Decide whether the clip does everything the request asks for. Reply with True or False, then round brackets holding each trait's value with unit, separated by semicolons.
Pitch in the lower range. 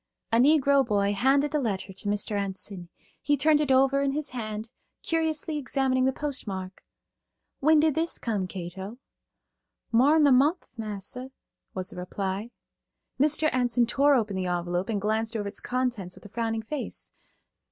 False (235 Hz)